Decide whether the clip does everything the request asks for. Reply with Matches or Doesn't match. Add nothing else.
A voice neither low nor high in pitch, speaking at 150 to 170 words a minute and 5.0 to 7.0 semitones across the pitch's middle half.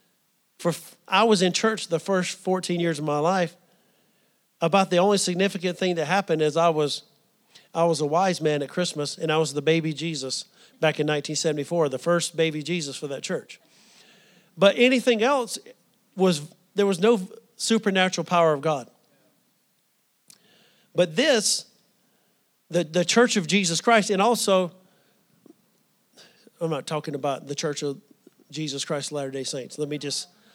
Doesn't match